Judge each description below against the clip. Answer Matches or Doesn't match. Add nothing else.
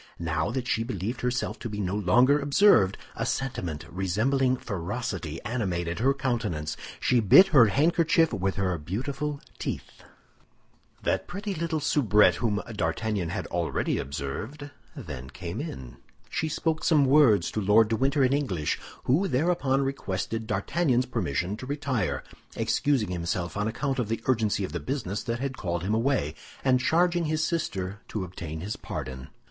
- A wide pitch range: Matches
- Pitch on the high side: Doesn't match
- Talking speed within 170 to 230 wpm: Doesn't match